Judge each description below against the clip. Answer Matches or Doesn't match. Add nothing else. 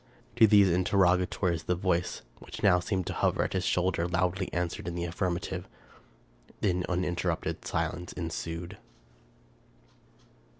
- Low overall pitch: Matches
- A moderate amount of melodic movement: Doesn't match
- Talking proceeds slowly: Matches